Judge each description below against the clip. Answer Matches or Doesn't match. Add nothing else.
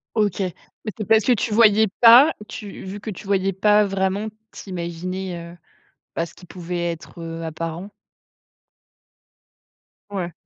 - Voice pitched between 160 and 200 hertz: Matches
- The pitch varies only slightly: Doesn't match